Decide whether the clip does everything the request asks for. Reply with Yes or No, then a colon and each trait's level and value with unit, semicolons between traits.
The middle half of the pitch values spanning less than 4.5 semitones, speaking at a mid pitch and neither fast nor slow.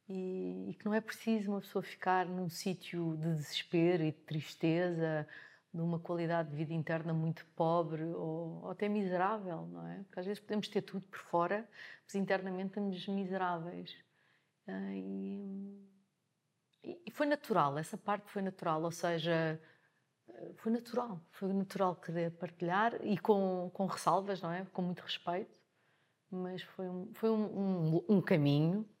Yes: average, 3.3 semitones; medium, 180 Hz; average, 145 wpm